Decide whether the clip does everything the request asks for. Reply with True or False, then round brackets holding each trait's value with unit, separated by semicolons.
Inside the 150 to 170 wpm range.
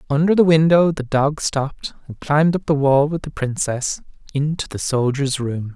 False (190 wpm)